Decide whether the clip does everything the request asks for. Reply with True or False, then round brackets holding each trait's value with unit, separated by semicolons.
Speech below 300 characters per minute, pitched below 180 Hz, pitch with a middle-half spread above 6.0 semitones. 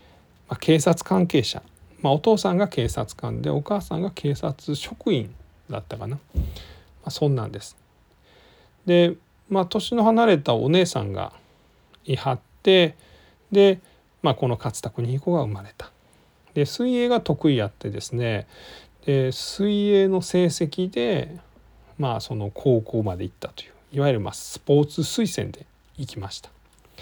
True (265 characters per minute; 140 Hz; 8.1 semitones)